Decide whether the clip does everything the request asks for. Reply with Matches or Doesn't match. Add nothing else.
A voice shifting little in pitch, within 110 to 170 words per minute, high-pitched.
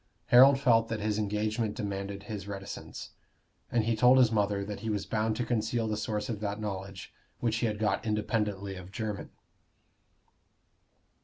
Doesn't match